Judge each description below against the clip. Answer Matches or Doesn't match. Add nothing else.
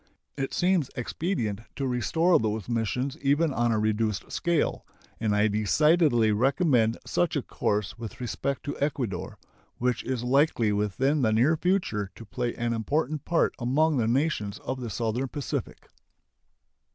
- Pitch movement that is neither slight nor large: Matches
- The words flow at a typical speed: Matches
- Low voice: Matches